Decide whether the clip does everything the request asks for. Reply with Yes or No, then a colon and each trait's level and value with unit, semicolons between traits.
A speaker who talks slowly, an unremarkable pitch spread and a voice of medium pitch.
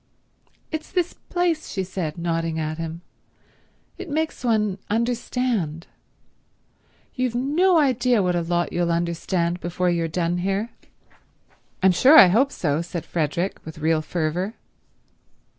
No: slow, 130 wpm; wide, 6.8 semitones; medium, 180 Hz